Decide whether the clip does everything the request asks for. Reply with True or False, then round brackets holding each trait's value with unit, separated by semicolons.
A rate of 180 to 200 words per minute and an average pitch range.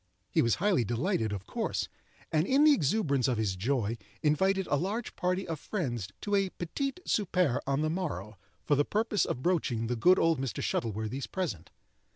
False (185 wpm; 8.1 semitones)